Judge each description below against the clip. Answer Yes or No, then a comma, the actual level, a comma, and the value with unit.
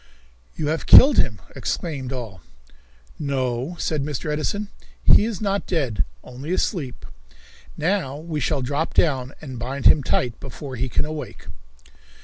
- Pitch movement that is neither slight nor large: Yes, average, 4.0 semitones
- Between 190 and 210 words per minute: No, average, 140 wpm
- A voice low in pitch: No, medium, 145 Hz